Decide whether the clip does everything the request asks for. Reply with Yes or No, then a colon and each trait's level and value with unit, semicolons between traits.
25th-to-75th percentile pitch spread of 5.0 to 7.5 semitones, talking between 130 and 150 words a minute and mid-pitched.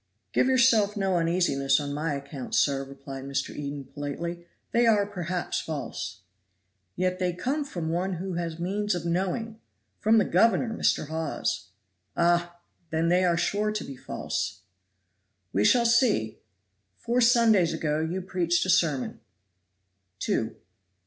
Yes: wide, 5.4 semitones; average, 140 wpm; medium, 175 Hz